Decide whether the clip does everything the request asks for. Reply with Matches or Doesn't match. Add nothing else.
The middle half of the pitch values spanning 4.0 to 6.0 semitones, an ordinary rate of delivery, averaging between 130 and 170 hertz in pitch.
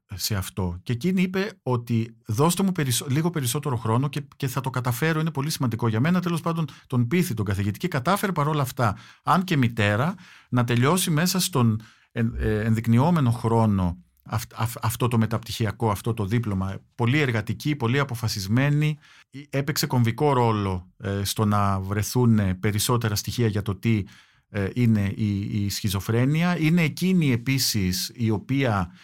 Doesn't match